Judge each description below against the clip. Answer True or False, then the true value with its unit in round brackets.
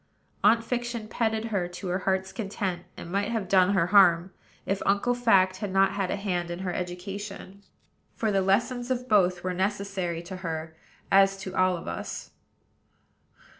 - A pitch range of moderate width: False (2.3 semitones)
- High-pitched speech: True (195 Hz)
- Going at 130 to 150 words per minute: False (170 wpm)